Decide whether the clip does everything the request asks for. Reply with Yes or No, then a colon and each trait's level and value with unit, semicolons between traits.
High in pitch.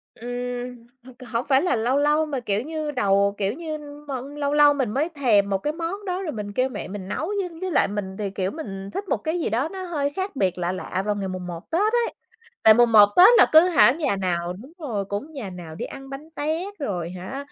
Yes: very high, 255 Hz